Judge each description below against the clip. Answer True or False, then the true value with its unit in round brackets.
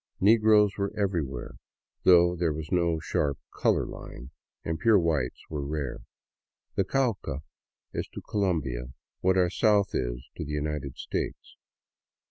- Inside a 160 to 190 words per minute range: False (140 wpm)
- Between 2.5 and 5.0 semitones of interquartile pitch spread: False (5.5 semitones)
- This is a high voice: False (85 Hz)